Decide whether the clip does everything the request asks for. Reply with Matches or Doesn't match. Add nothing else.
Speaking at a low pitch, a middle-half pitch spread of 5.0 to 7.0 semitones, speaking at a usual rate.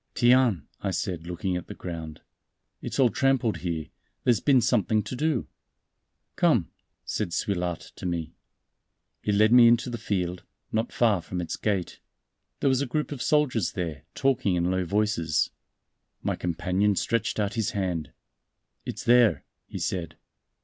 Matches